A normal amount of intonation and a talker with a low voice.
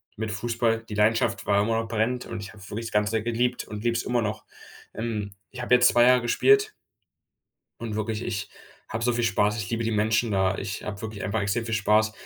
No: narrow, 2.0 semitones; low, 110 Hz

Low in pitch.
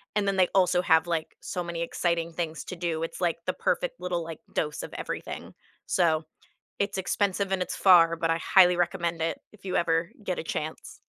No: medium, 170 Hz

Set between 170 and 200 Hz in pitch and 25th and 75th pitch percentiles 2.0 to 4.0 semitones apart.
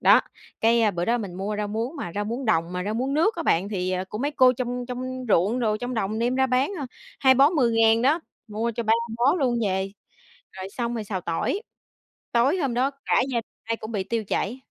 No: high, 235 Hz; average, 3.7 semitones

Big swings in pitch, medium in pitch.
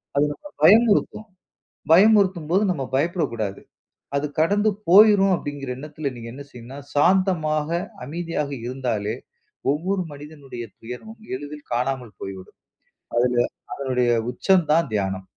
Yes: wide, 6.5 semitones; medium, 150 Hz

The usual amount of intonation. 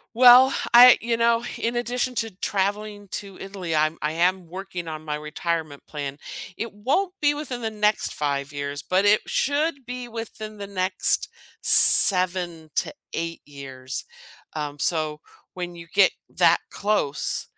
No: wide, 6.6 semitones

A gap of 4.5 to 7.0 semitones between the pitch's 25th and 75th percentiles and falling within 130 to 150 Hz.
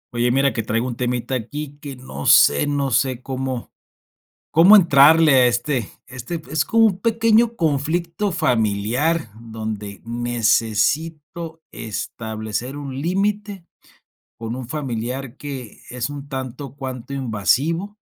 Yes: average, 5.2 semitones; low, 135 Hz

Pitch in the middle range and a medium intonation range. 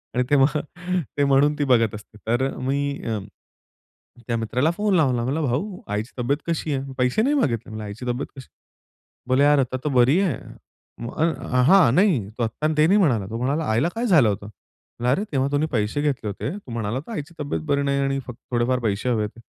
No: low, 130 Hz; average, 4.1 semitones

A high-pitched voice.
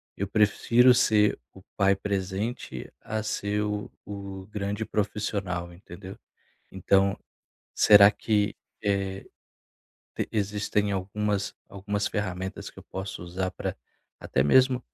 No: low, 100 Hz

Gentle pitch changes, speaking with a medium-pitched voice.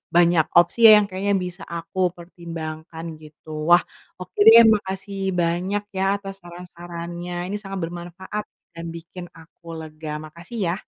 Yes: narrow, 2.2 semitones; medium, 175 Hz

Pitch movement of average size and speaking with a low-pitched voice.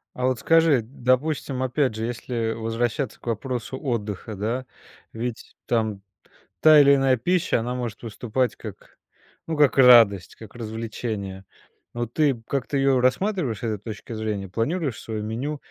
Yes: average, 3.4 semitones; low, 120 Hz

